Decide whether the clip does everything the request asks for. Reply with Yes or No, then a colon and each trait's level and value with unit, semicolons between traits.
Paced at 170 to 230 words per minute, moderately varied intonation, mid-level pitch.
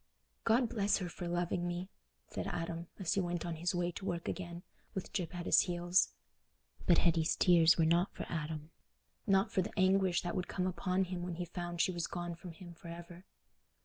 No: fast, 205 wpm; narrow, 1.4 semitones; medium, 175 Hz